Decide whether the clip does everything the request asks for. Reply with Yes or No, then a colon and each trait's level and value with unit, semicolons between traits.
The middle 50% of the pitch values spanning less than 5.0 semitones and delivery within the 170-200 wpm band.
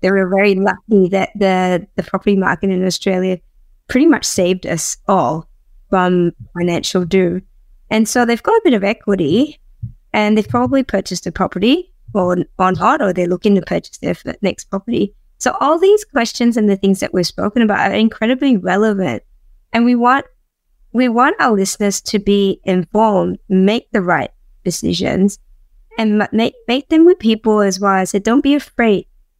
Yes: average, 3.9 semitones; average, 175 wpm